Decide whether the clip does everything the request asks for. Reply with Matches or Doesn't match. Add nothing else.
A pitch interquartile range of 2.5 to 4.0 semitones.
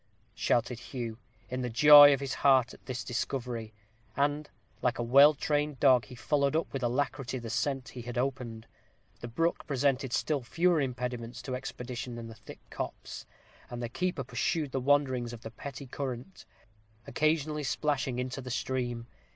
Matches